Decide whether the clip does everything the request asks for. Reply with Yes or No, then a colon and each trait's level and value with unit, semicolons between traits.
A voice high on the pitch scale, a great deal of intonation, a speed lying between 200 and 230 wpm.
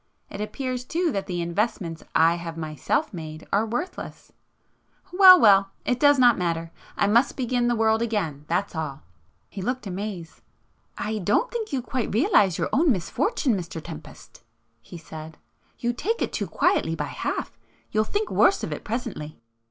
No: high, 205 Hz; wide, 7.0 semitones; average, 150 wpm